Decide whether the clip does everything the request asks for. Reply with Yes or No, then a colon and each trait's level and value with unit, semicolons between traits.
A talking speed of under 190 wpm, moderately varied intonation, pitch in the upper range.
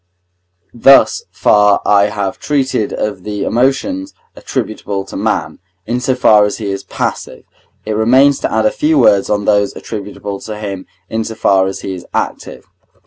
No: average, 170 wpm; average, 3.7 semitones; low, 105 Hz